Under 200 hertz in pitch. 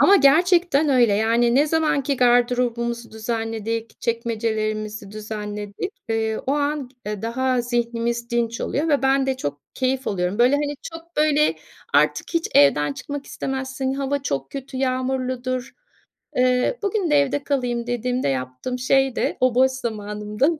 No: very high, 250 Hz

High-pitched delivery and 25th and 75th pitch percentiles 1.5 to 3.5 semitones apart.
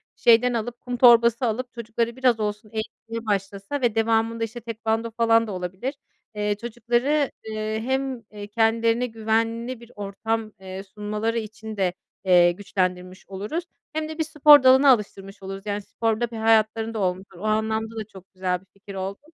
Yes: high, 225 Hz; narrow, 2.5 semitones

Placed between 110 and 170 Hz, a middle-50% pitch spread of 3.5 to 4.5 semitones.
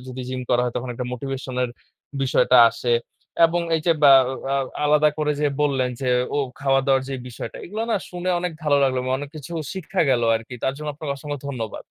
No: low, 135 Hz; average, 2.8 semitones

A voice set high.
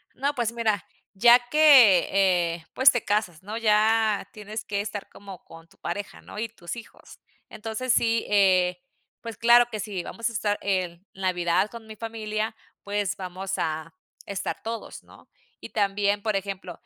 Yes: high, 205 Hz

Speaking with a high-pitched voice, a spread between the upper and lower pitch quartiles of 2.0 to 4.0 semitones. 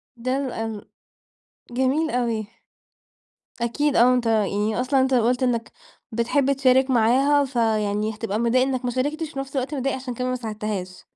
Yes: very high, 250 Hz; average, 3.0 semitones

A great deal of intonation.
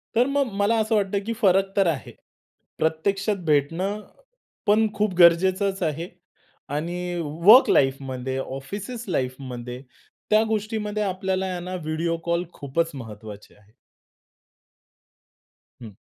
Yes: wide, 6.3 semitones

